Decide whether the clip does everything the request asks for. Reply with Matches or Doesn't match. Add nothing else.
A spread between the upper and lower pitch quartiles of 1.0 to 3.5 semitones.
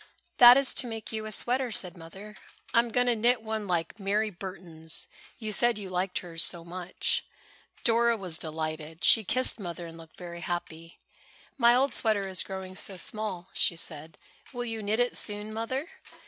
Doesn't match